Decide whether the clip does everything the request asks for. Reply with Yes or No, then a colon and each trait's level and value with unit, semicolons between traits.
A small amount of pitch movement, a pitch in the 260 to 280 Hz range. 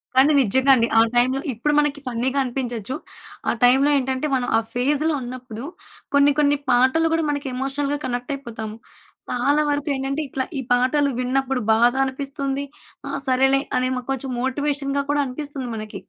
Yes: narrow, 2.3 semitones; very high, 265 Hz